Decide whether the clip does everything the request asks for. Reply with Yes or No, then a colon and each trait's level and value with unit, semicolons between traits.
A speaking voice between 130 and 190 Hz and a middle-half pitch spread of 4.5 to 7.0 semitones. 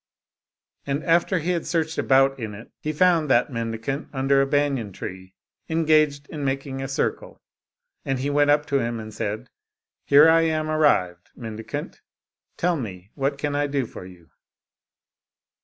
Yes: medium, 140 Hz; average, 4.8 semitones